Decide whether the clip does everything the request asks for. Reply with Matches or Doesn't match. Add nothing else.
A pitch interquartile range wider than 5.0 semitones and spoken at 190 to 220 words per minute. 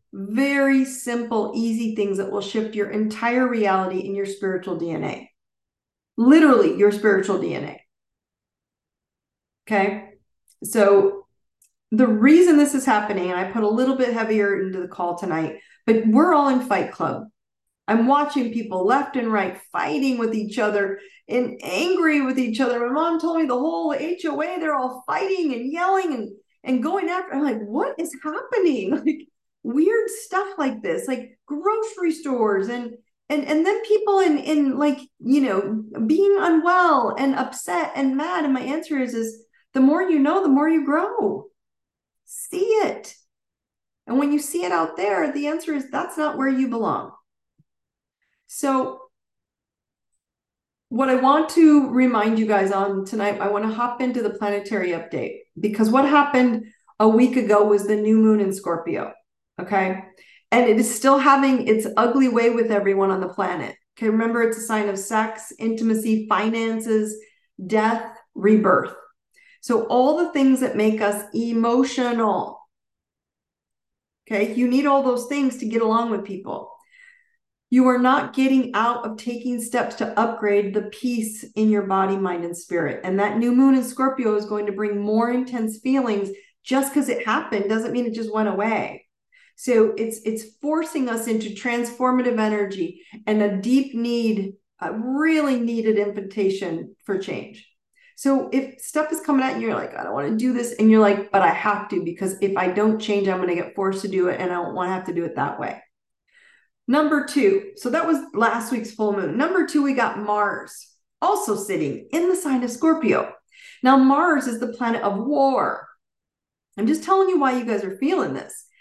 Doesn't match